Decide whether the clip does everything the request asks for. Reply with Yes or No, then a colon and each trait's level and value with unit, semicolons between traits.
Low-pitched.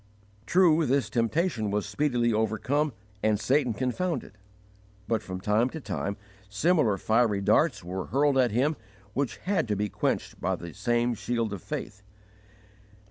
Yes: low, 120 Hz